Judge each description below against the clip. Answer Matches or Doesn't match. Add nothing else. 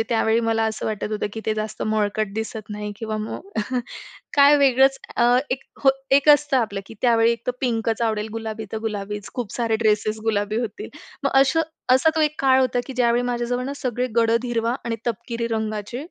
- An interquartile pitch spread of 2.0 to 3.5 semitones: Matches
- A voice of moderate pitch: Doesn't match